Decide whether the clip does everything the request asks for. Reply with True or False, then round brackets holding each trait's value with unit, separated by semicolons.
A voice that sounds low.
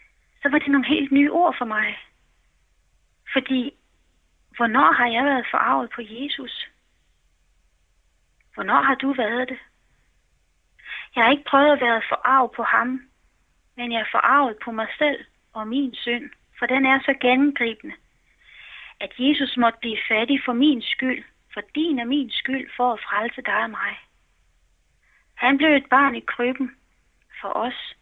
False (255 Hz)